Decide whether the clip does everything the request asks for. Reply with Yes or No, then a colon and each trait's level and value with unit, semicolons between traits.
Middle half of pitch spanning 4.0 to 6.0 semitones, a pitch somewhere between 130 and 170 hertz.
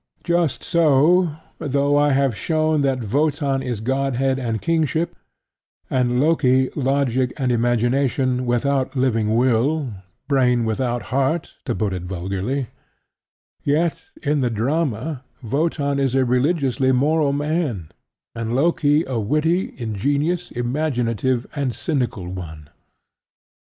No: average, 3.5 semitones; low, 135 Hz